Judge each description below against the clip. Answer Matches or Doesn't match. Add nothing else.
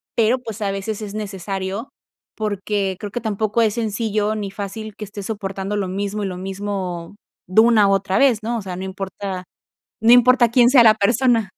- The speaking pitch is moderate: Doesn't match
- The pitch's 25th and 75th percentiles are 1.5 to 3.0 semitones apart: Matches